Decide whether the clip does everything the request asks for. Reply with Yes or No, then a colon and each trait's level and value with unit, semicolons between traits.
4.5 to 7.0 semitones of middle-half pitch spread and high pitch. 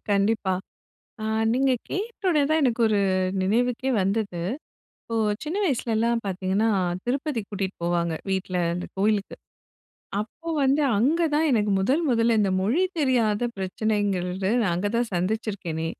Yes: average, 5.1 semitones; high, 220 Hz